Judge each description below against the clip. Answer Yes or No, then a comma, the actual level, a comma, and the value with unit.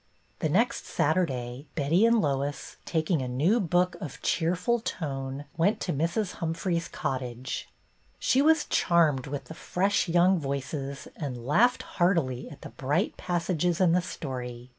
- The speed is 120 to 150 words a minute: Yes, average, 145 wpm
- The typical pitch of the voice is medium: Yes, medium, 160 Hz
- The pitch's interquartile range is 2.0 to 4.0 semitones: No, average, 4.8 semitones